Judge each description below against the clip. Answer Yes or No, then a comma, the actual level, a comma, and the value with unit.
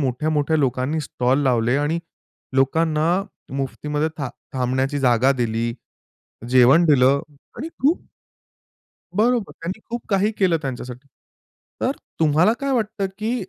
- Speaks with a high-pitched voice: No, medium, 145 Hz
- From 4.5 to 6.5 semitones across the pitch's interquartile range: Yes, wide, 5.5 semitones